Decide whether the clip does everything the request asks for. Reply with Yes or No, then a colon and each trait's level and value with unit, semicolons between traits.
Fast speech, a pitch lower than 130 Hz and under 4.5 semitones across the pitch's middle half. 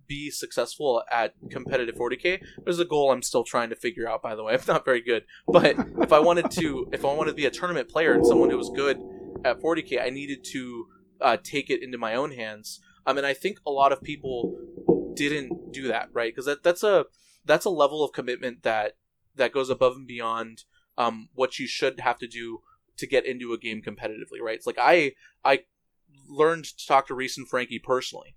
No: fast, 220 wpm; low, 135 Hz; average, 3.9 semitones